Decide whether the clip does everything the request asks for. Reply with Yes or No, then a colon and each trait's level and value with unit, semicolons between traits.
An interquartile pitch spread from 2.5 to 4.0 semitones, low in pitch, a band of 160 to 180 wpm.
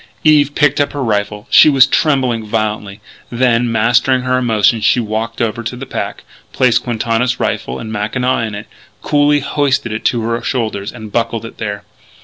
Yes: average, 2.8 semitones; low, 115 Hz; average, 175 wpm